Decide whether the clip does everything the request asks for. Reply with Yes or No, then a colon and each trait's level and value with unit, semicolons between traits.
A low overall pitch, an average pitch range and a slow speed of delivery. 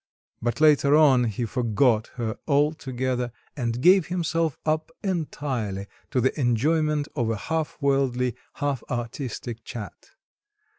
Yes: low, 130 Hz; average, 4.2 semitones; slow, 120 wpm